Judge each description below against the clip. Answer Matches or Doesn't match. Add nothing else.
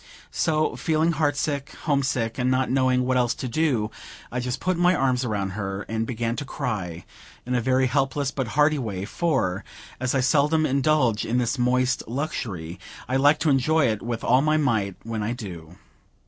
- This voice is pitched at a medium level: Doesn't match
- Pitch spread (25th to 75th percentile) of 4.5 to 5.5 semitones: Doesn't match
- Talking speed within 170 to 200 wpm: Matches